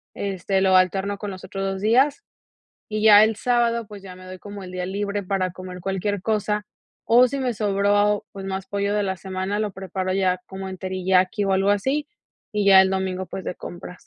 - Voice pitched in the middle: No, high, 195 Hz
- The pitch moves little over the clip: Yes, narrow, 1.7 semitones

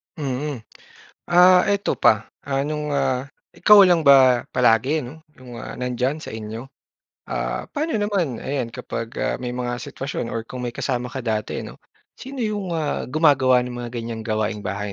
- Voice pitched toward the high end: No, low, 130 Hz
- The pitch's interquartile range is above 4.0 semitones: Yes, average, 4.6 semitones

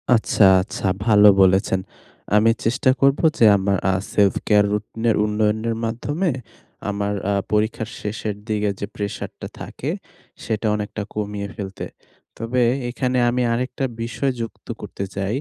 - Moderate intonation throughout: No, narrow, 2.2 semitones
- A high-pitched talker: No, low, 105 Hz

